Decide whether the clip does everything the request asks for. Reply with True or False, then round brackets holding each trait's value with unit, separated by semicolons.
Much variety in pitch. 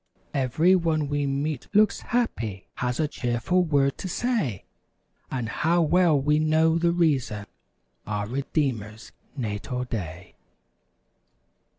True (5.7 semitones)